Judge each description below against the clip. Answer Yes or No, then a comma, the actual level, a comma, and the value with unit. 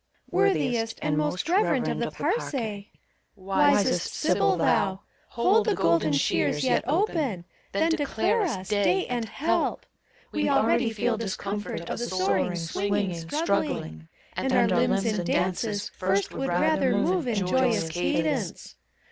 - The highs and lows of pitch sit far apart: Yes, wide, 6.2 semitones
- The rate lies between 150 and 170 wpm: No, slow, 135 wpm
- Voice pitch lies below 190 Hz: No, high, 205 Hz